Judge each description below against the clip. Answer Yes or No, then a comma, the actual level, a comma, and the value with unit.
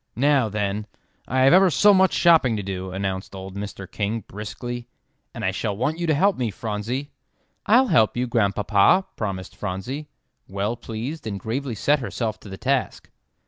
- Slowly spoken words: No, average, 175 wpm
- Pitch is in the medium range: No, low, 115 Hz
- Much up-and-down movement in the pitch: Yes, wide, 5.7 semitones